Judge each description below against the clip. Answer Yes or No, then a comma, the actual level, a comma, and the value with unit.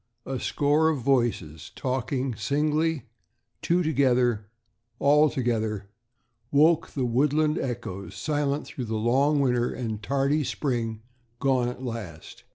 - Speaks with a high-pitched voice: No, low, 130 Hz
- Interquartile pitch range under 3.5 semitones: No, average, 4.0 semitones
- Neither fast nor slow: No, slow, 120 wpm